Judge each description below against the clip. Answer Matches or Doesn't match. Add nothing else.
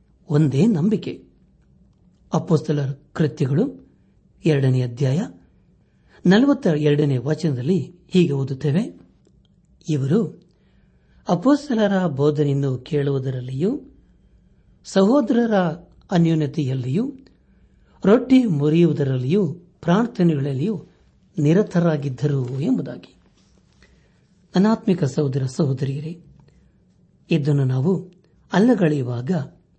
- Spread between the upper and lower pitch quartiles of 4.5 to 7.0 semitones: Matches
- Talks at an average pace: Doesn't match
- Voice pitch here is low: Doesn't match